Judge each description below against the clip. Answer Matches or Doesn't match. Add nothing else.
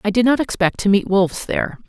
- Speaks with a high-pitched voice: Matches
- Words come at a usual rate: Doesn't match